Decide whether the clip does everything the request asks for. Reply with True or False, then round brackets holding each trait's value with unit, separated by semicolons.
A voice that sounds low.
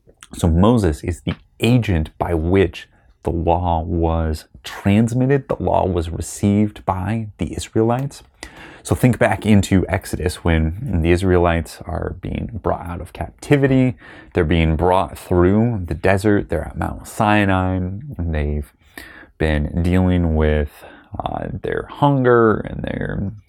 True (90 Hz)